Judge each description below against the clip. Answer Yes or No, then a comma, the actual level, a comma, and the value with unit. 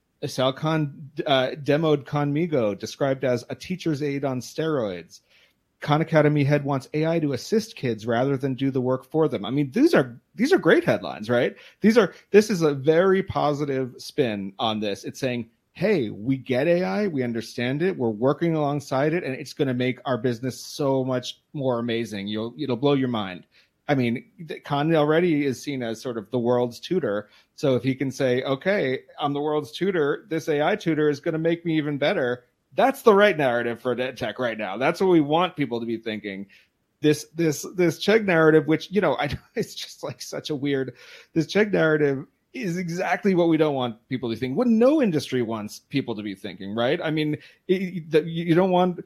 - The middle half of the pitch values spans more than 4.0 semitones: Yes, average, 4.5 semitones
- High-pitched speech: No, medium, 145 Hz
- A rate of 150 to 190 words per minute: No, fast, 205 wpm